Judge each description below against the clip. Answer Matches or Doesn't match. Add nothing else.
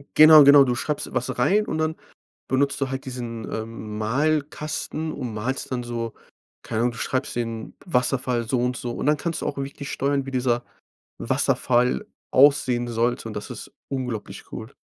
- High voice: Doesn't match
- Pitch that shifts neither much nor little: Matches